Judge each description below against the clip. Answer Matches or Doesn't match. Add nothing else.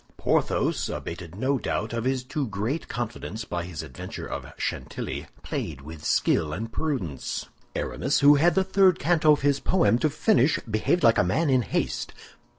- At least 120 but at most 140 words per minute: Doesn't match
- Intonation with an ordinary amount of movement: Doesn't match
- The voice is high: Doesn't match